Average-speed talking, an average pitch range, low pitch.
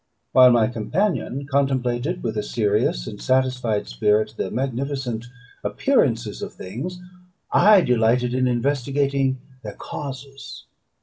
No: slow, 115 wpm; average, 3.5 semitones; low, 125 Hz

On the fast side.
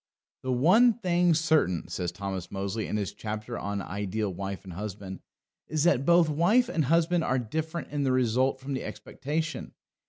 No: average, 175 wpm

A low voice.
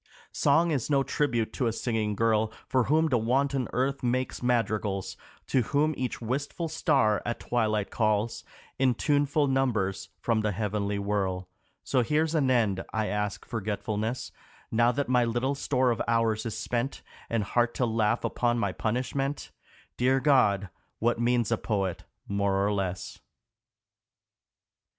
Yes: low, 115 Hz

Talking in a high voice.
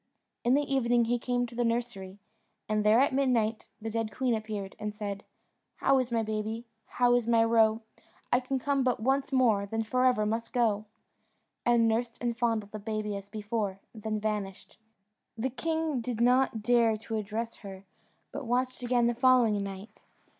Yes: high, 230 Hz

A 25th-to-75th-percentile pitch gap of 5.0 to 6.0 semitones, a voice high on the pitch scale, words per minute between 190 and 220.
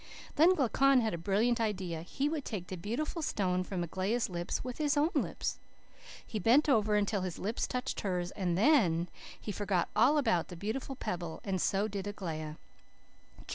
No: wide, 5.6 semitones; high, 205 Hz; average, 175 wpm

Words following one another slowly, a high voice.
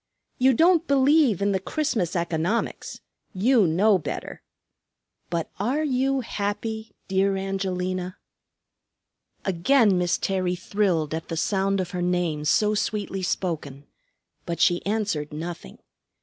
Yes: slow, 120 wpm; high, 195 Hz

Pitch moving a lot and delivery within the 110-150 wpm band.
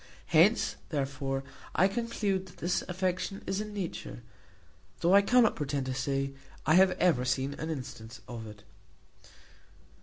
Yes: wide, 6.1 semitones; average, 145 wpm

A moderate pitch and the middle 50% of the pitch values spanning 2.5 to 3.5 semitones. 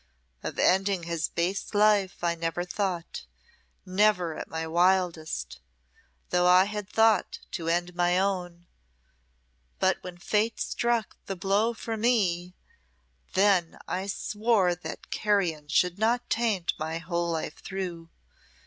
Yes: medium, 180 Hz; average, 3.2 semitones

